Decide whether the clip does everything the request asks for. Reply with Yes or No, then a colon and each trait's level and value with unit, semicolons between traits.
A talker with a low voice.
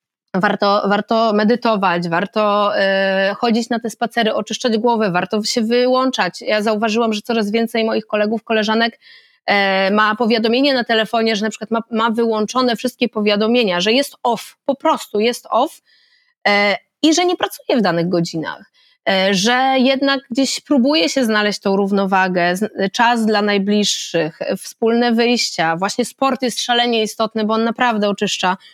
No: high, 225 Hz